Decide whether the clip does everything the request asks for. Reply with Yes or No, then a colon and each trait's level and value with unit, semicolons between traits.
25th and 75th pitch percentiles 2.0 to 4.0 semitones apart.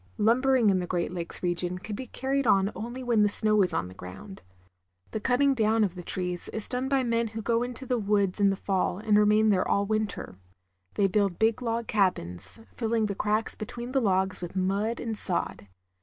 Yes: average, 3.6 semitones